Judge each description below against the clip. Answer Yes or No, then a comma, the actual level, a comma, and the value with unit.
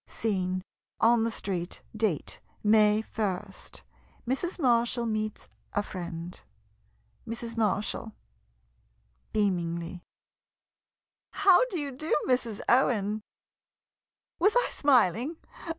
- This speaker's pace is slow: Yes, slow, 100 wpm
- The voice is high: Yes, high, 220 Hz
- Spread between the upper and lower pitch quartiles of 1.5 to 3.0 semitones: No, average, 4.3 semitones